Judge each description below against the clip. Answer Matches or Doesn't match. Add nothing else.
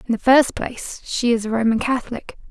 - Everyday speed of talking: Doesn't match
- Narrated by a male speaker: Doesn't match